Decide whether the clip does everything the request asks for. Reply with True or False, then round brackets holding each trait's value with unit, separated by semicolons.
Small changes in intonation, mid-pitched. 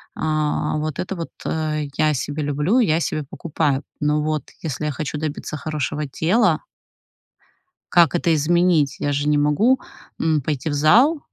True (2.0 semitones; 155 Hz)